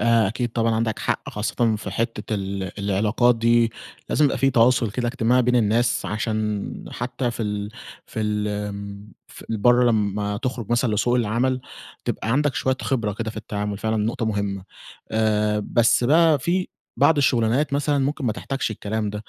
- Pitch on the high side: No, low, 115 Hz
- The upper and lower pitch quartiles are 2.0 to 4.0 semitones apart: Yes, average, 2.8 semitones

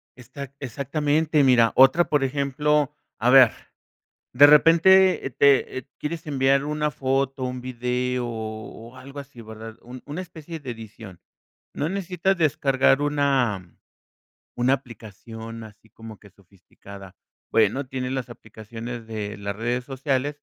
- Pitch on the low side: Yes, low, 130 Hz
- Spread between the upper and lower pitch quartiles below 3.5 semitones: No, average, 4.2 semitones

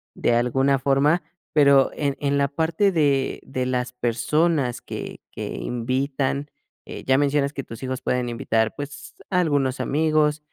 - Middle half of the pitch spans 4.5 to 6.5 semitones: No, narrow, 2.6 semitones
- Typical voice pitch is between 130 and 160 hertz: Yes, medium, 140 Hz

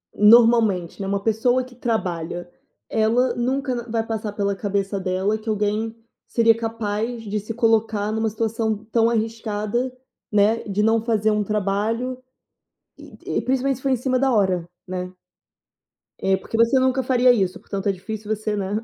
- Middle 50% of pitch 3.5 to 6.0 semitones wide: No, narrow, 2.4 semitones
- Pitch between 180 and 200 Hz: No, high, 220 Hz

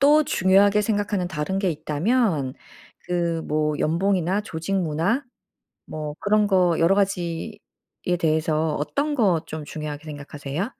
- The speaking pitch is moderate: Yes, medium, 170 Hz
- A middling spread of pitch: Yes, average, 4.6 semitones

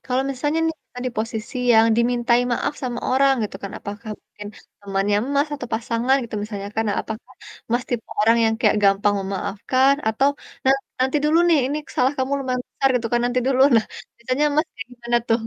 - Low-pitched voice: No, high, 240 Hz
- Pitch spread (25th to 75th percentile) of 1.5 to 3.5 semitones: Yes, average, 3.1 semitones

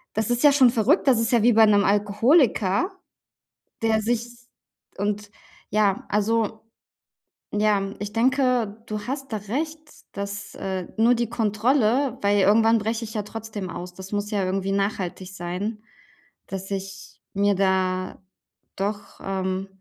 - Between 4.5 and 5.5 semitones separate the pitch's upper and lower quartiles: No, average, 2.7 semitones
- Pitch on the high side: Yes, high, 210 Hz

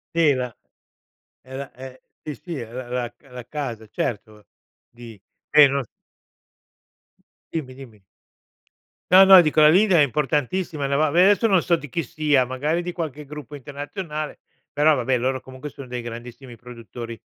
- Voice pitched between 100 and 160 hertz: Yes, medium, 140 Hz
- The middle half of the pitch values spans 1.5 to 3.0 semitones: No, average, 3.8 semitones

